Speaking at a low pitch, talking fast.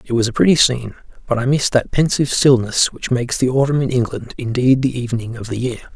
Yes: low, 125 Hz; fast, 230 wpm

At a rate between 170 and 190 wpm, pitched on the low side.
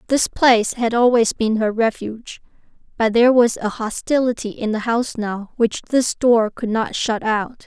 No: average, 180 wpm; high, 230 Hz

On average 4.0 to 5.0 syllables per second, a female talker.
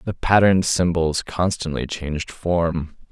No: 4.2 syllables/s; male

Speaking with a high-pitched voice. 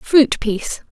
Yes: very high, 250 Hz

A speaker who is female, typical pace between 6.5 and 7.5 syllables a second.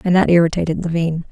Yes: female; 6.8 syllables/s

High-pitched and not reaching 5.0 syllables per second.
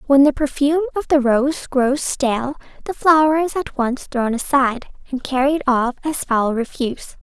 Yes: very high, 275 Hz; 4.7 syllables/s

